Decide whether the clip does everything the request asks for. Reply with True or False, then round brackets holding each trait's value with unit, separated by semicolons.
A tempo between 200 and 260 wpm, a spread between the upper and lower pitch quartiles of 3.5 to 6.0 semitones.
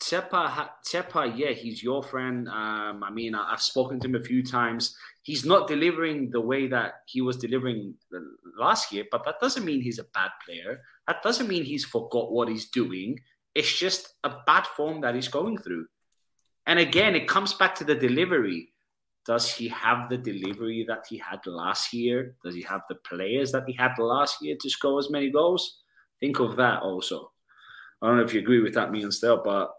True (205 wpm; 3.8 semitones)